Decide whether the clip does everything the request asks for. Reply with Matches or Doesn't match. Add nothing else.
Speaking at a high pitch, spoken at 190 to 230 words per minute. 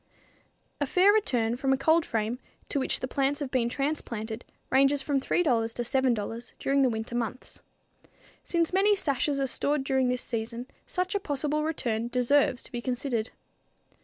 Doesn't match